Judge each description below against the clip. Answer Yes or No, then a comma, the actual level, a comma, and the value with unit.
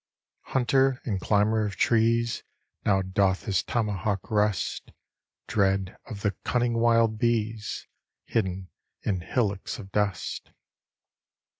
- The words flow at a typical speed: No, slow, 110 wpm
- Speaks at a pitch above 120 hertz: No, low, 105 Hz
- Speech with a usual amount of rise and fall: Yes, average, 3.0 semitones